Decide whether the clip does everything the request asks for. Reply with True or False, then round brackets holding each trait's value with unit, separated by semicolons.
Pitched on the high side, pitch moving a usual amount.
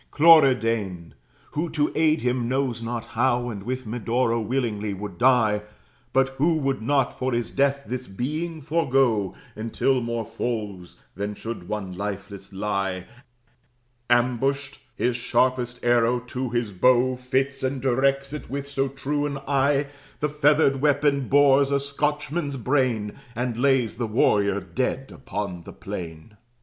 False (125 Hz; 3.8 semitones)